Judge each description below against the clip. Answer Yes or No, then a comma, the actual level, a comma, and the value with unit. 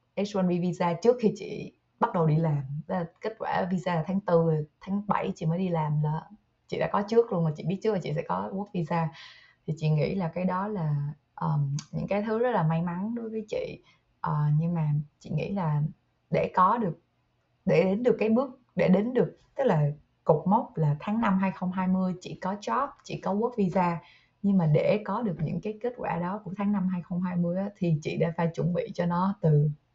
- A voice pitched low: No, medium, 180 Hz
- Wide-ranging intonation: No, average, 3.9 semitones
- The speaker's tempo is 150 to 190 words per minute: No, average, 225 wpm